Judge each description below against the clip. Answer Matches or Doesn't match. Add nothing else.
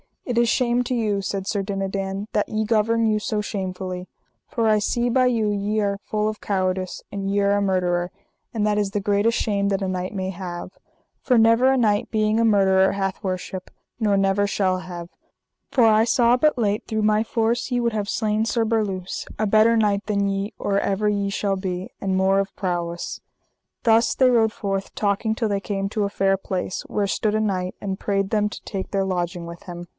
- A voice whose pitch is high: Matches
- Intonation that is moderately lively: Doesn't match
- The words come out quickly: Matches